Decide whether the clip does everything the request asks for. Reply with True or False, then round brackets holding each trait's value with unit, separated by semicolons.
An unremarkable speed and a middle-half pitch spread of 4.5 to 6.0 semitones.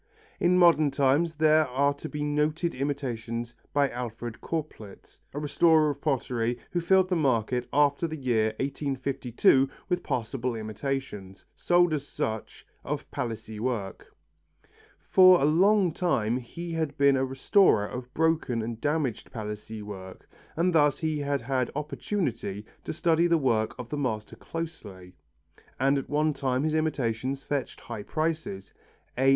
True (145 wpm; 5.0 semitones)